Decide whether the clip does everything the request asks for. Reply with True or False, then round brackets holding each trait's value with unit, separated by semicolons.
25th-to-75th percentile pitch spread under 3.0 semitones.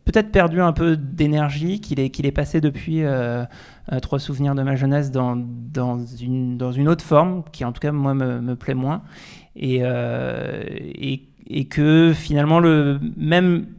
False (3.8 semitones)